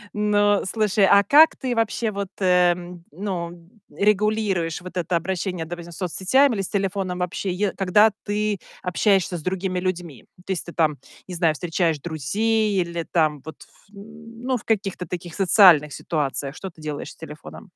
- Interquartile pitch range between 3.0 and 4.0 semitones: Yes, average, 3.4 semitones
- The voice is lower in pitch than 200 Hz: Yes, medium, 185 Hz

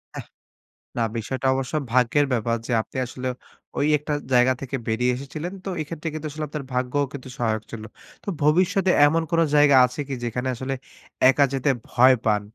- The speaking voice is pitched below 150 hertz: Yes, low, 135 Hz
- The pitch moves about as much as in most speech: Yes, average, 3.3 semitones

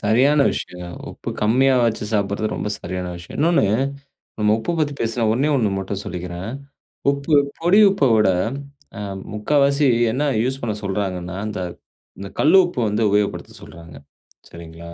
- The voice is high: No, low, 110 Hz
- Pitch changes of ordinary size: No, wide, 6.5 semitones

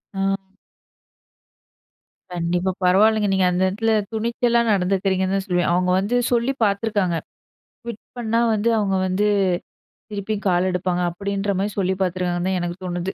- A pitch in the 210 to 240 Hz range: No, high, 190 Hz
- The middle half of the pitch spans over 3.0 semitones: No, narrow, 2.6 semitones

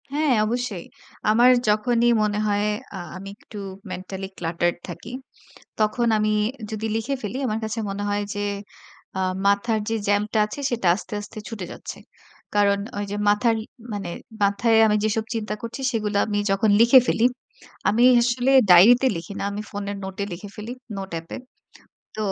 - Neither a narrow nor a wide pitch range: No, narrow, 2.3 semitones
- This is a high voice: Yes, high, 210 Hz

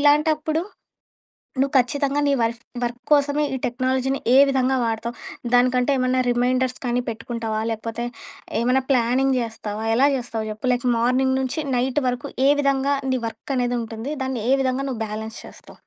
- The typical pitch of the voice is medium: No, very high, 255 Hz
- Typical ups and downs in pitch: No, narrow, 2.3 semitones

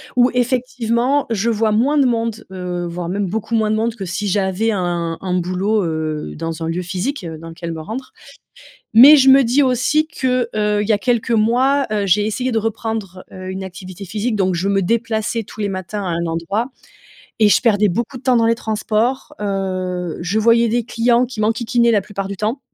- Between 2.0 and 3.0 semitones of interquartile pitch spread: No, average, 4.0 semitones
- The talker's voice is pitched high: Yes, high, 215 Hz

